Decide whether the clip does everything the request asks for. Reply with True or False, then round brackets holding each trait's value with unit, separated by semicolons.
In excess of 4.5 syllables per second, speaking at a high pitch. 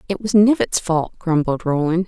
False (4.9 syllables/s; 180 Hz)